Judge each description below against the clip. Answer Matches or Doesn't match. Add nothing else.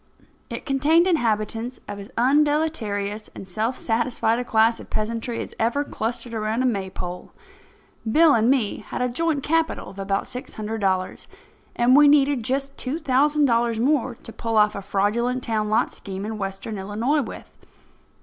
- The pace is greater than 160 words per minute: Matches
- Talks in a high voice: Matches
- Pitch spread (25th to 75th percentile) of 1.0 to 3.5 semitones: Doesn't match